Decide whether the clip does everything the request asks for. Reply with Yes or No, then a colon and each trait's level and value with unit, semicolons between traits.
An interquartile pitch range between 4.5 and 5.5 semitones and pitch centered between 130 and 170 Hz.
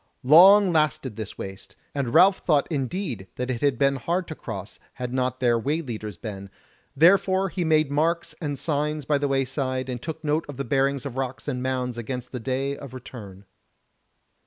No: average, 3.6 semitones; low, 135 Hz